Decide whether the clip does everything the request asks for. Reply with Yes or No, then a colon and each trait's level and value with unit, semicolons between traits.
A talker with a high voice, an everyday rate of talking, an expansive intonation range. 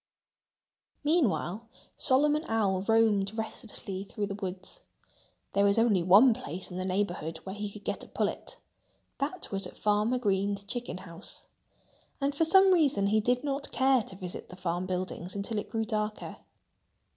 No: high, 210 Hz; average, 160 wpm; average, 4.3 semitones